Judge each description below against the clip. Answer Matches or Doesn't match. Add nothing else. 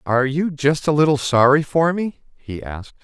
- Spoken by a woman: Doesn't match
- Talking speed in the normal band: Matches